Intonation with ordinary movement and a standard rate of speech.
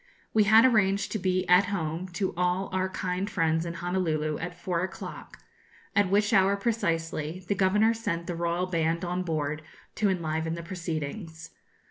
Yes: average, 3.0 semitones; average, 165 wpm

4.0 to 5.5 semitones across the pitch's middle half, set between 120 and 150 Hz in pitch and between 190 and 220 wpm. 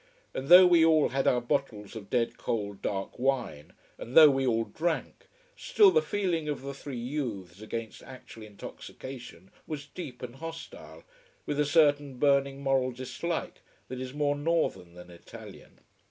No: average, 4.3 semitones; low, 135 Hz; average, 160 wpm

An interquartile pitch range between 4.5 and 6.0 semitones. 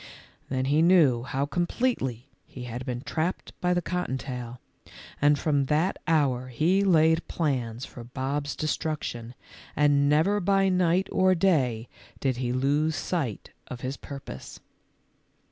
Yes: average, 5.0 semitones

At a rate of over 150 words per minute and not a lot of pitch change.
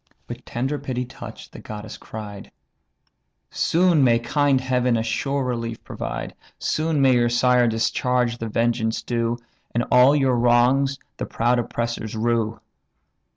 No: average, 140 wpm; narrow, 2.0 semitones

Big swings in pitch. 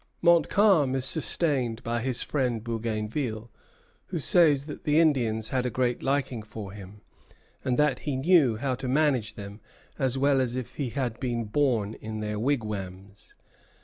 No: average, 4.5 semitones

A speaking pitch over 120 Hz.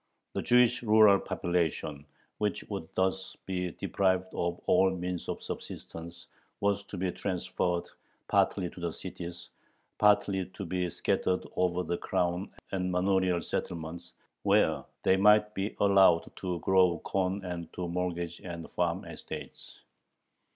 No: very low, 90 Hz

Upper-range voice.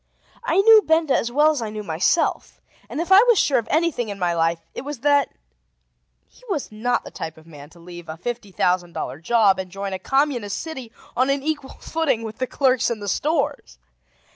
Yes: high, 235 Hz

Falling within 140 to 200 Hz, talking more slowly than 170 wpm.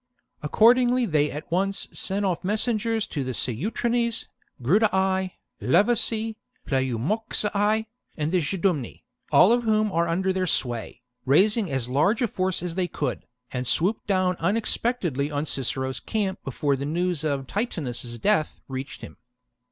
Yes: medium, 185 Hz; average, 145 wpm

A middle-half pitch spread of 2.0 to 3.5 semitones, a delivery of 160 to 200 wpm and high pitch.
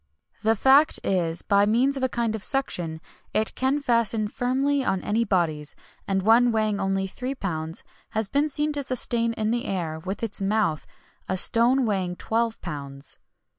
No: average, 4.8 semitones; average, 185 wpm; high, 220 Hz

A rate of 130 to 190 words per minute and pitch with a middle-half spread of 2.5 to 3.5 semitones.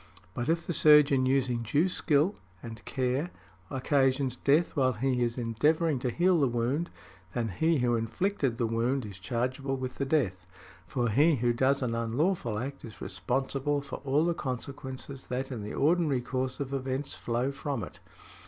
Yes: average, 170 wpm; average, 3.1 semitones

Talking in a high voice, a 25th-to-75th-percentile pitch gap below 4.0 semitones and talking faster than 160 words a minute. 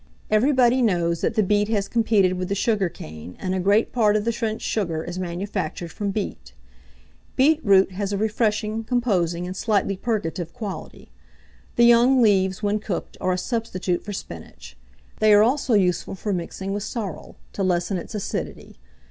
Yes: high, 205 Hz; average, 3.3 semitones; average, 170 wpm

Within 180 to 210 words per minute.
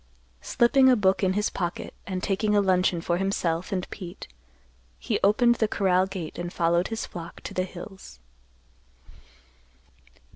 No: average, 150 wpm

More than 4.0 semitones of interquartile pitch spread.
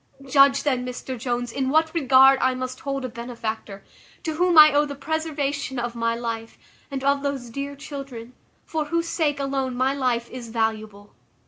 No: average, 2.9 semitones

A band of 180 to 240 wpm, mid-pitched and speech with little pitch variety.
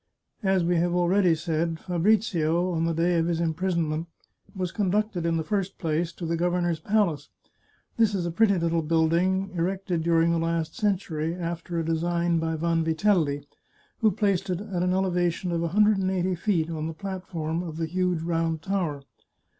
Yes: average, 185 wpm; medium, 170 Hz; narrow, 2.3 semitones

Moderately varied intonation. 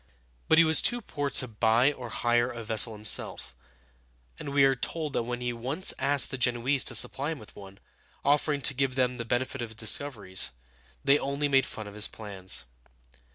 Yes: average, 3.9 semitones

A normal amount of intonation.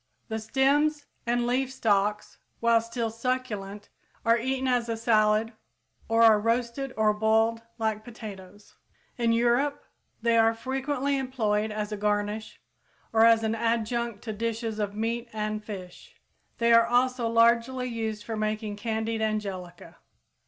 No: narrow, 1.9 semitones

